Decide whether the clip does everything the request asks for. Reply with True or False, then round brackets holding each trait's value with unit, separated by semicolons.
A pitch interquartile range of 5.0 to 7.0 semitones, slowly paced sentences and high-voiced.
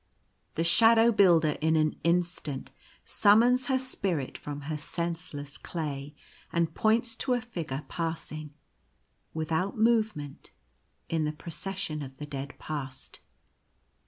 False (5.5 semitones; 120 wpm; 165 Hz)